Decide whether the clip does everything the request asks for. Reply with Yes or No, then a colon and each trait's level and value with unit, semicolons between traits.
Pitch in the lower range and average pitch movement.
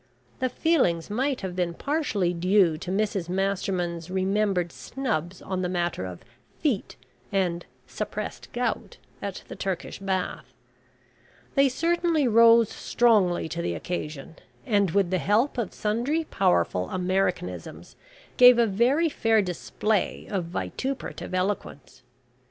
No: high, 195 Hz; average, 5.0 semitones